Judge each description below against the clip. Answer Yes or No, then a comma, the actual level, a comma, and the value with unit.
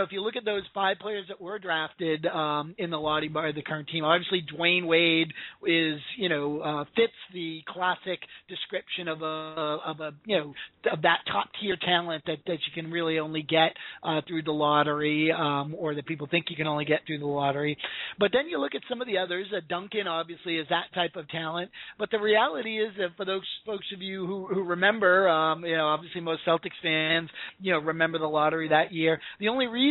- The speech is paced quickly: Yes, fast, 225 wpm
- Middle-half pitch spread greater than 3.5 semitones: No, average, 3.2 semitones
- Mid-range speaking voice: Yes, medium, 165 Hz